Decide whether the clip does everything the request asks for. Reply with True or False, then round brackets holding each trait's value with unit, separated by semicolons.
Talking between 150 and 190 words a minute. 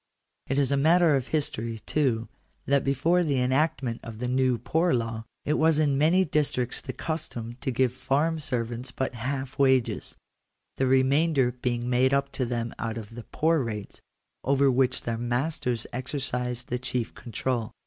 True (165 wpm)